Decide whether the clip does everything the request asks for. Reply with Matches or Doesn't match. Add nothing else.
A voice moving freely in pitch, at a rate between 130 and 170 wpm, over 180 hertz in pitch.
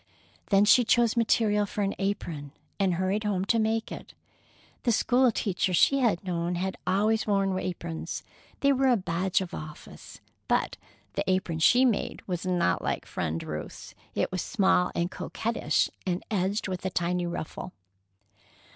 Doesn't match